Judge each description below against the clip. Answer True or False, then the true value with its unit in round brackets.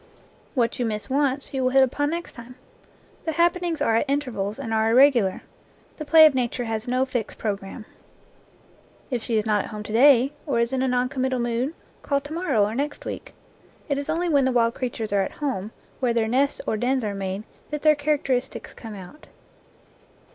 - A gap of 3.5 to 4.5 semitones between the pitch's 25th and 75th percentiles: True (4.1 semitones)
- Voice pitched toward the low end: False (255 Hz)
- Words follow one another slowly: False (205 wpm)